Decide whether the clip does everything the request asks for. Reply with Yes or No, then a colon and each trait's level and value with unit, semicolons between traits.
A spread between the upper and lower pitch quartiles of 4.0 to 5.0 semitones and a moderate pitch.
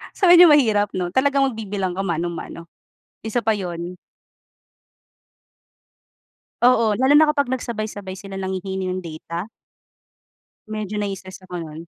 No: average, 4.4 semitones; high, 200 Hz